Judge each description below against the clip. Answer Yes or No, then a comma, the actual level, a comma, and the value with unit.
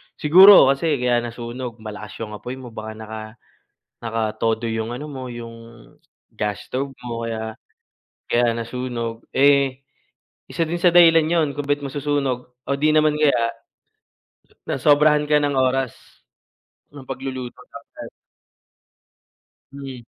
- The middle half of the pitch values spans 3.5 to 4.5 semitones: Yes, average, 3.9 semitones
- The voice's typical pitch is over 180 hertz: No, low, 130 Hz